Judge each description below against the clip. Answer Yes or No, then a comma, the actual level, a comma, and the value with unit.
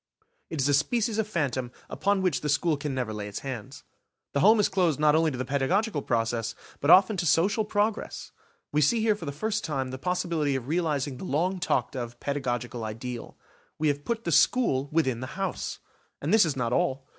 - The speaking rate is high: Yes, fast, 210 wpm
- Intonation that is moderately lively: No, wide, 6.1 semitones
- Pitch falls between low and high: Yes, medium, 150 Hz